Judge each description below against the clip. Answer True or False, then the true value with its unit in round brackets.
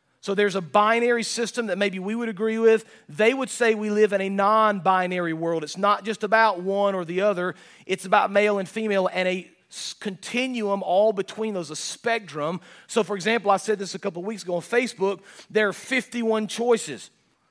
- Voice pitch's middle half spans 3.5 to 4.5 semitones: False (2.7 semitones)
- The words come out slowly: False (200 wpm)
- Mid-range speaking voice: False (205 Hz)